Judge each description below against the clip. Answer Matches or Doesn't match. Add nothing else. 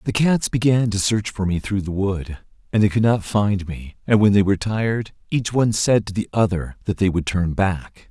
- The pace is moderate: Doesn't match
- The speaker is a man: Matches